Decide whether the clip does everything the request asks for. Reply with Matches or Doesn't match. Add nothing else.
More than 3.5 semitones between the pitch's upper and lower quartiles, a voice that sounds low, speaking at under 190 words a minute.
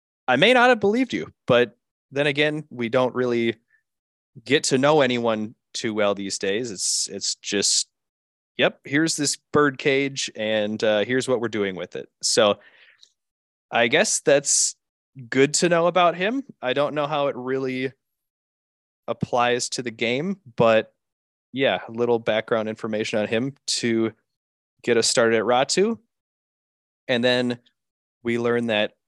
Matches